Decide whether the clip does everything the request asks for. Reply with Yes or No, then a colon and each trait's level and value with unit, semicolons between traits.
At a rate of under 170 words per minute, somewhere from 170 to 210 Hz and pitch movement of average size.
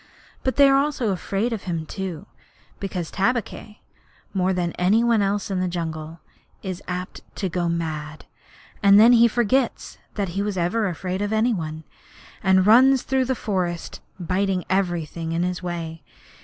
Yes: average, 160 wpm; high, 190 Hz; average, 4.0 semitones